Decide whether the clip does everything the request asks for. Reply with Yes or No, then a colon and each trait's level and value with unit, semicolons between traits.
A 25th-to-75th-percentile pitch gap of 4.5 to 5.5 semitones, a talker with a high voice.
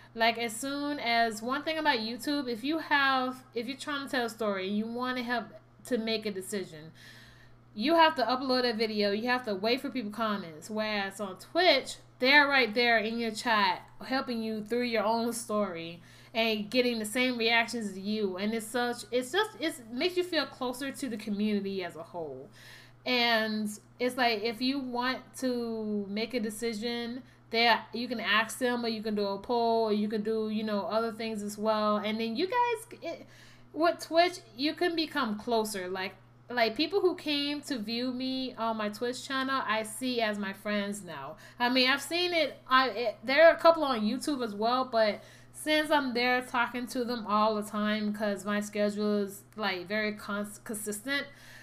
No: average, 3.5 semitones; high, 230 Hz